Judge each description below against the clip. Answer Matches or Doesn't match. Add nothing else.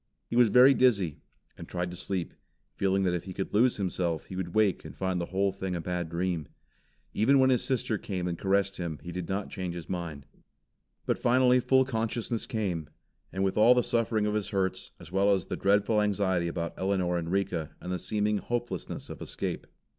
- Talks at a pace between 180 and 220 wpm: Matches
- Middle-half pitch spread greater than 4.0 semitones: Doesn't match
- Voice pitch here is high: Doesn't match